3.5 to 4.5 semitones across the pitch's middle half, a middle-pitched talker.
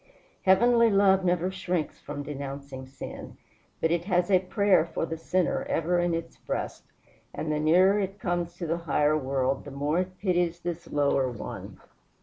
Yes: average, 3.8 semitones; medium, 170 Hz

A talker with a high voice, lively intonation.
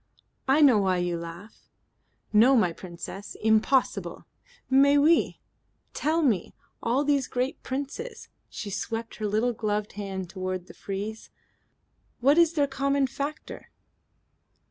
Yes: high, 230 Hz; wide, 6.0 semitones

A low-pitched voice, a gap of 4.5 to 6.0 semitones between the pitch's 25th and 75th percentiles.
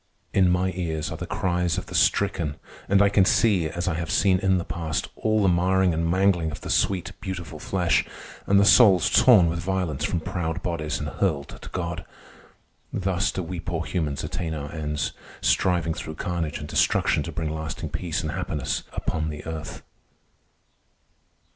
No: very low, 85 Hz; average, 2.9 semitones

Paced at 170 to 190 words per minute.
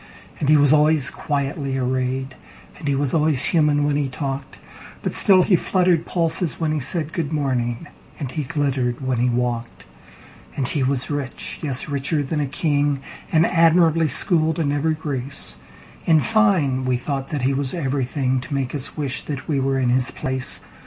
No: average, 160 wpm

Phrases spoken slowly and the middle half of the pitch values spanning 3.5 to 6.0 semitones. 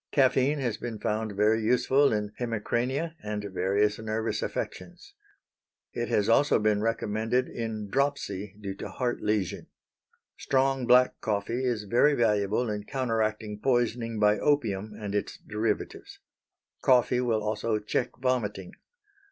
No: slow, 130 wpm; average, 3.0 semitones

